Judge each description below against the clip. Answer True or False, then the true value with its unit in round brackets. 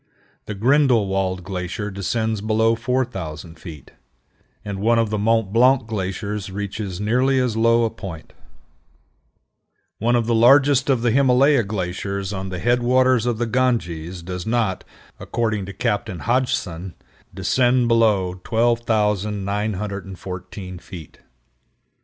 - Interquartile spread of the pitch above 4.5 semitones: False (3.8 semitones)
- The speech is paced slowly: True (125 wpm)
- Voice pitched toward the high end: False (105 Hz)